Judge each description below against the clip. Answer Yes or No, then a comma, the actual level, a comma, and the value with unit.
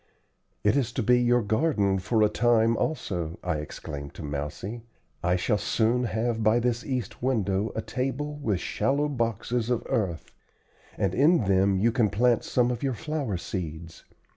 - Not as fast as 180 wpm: Yes, average, 165 wpm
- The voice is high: No, low, 115 Hz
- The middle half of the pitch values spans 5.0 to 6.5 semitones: No, average, 4.3 semitones